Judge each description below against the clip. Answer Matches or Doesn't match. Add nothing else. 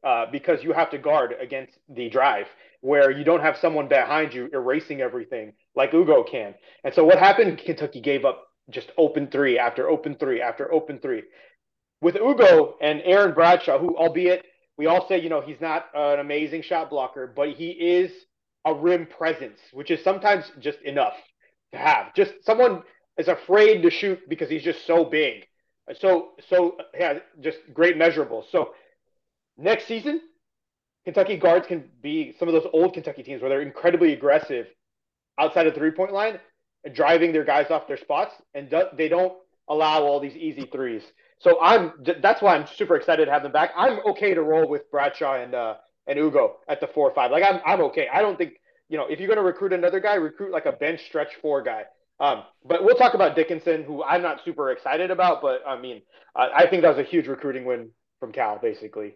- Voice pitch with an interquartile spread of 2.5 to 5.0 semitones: Doesn't match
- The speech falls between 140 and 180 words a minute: Doesn't match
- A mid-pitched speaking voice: Matches